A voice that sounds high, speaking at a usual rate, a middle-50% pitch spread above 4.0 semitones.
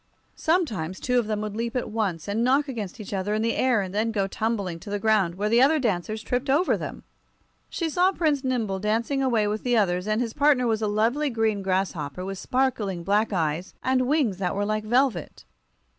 No: high, 220 Hz; fast, 215 wpm; average, 4.4 semitones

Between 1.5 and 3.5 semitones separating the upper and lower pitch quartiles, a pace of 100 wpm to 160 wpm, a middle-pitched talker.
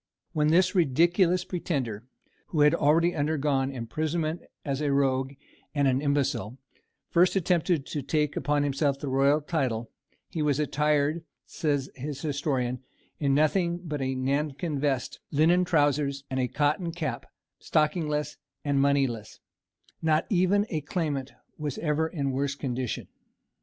Yes: average, 2.7 semitones; slow, 135 wpm; medium, 145 Hz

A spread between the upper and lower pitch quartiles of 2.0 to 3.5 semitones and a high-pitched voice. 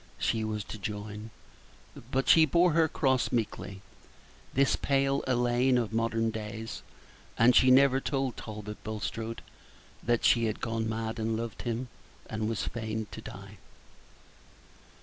No: average, 2.9 semitones; low, 115 Hz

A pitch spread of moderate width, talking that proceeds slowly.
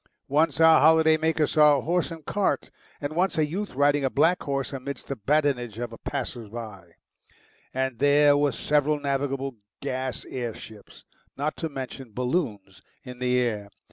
No: average, 3.5 semitones; average, 165 wpm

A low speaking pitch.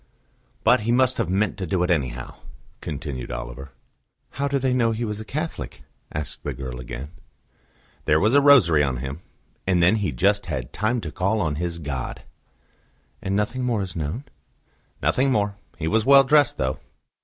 Yes: very low, 95 Hz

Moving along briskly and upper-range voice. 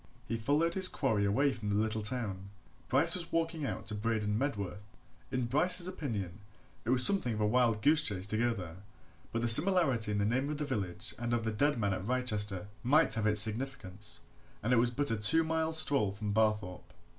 No: fast, 210 wpm; low, 115 Hz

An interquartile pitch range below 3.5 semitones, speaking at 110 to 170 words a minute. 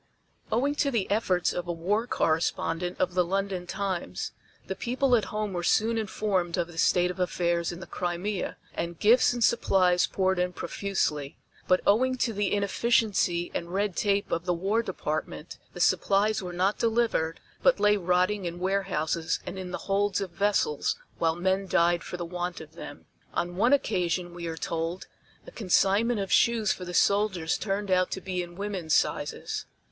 No: average, 2.9 semitones; average, 180 wpm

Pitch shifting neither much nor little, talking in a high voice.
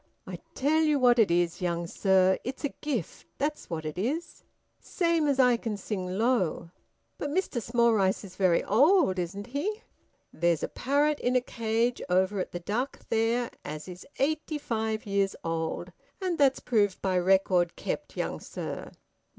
No: wide, 6.8 semitones; high, 220 Hz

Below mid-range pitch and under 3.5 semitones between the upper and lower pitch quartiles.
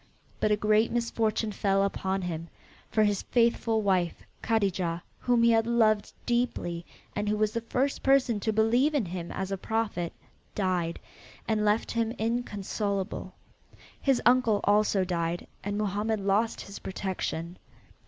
No: high, 210 Hz; average, 3.0 semitones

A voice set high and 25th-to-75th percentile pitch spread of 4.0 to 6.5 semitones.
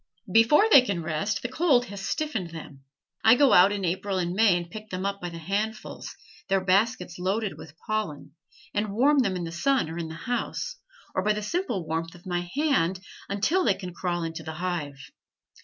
Yes: high, 195 Hz; average, 4.6 semitones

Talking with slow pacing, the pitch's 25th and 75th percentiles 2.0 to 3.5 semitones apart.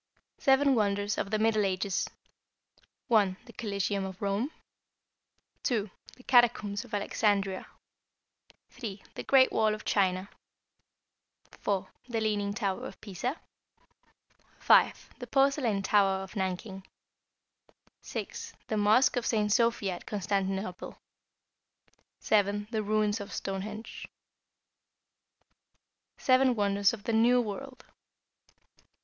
Yes: slow, 110 wpm; average, 2.8 semitones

